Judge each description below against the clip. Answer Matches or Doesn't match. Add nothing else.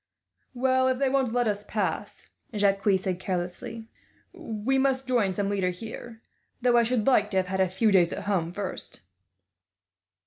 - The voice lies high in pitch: Matches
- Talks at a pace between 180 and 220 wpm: Doesn't match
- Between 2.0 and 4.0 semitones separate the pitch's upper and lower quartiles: Doesn't match